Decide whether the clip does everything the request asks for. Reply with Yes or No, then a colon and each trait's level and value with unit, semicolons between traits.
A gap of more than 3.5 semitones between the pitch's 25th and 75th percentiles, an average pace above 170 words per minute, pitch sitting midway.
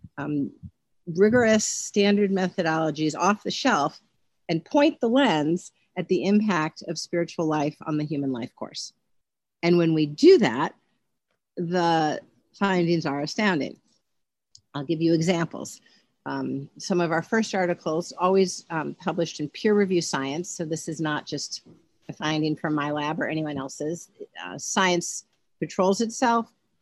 No: average, 3.9 semitones; average, 145 wpm; medium, 170 Hz